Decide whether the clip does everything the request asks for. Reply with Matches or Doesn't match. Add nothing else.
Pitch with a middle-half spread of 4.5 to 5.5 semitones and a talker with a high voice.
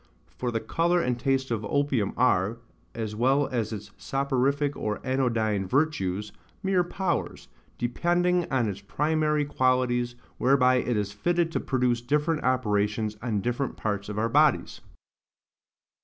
Doesn't match